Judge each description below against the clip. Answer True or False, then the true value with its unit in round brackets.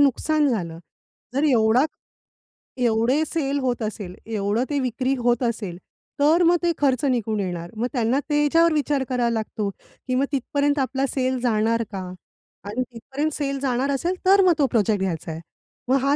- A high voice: True (255 Hz)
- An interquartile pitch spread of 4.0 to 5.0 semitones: True (4.3 semitones)